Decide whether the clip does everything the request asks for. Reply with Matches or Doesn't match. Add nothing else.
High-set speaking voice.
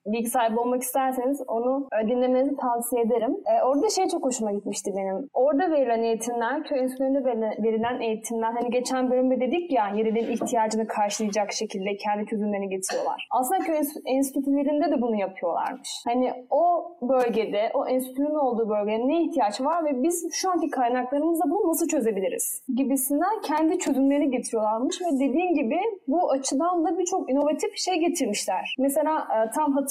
Matches